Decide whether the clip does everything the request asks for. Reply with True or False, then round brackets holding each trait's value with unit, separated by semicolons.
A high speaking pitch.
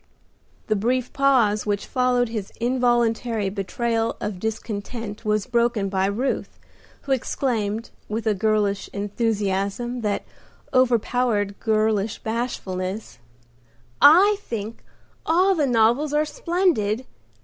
True (225 Hz)